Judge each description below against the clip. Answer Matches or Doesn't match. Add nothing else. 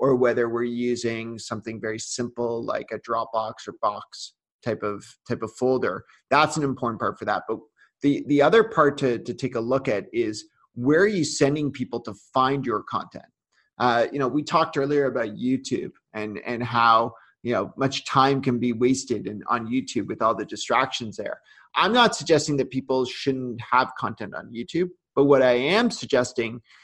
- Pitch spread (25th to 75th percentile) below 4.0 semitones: Matches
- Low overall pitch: Matches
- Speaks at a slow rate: Doesn't match